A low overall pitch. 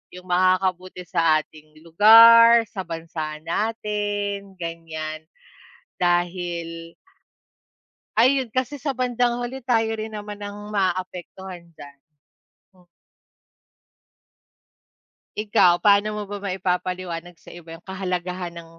No: medium, 185 Hz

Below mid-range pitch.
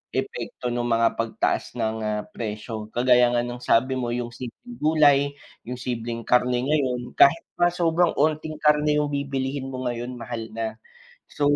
Yes: low, 125 Hz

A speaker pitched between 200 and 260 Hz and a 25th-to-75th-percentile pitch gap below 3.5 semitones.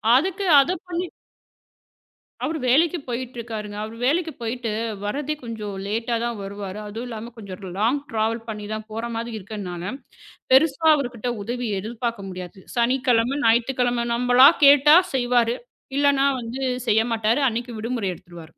Yes: high, 235 Hz; average, 3.1 semitones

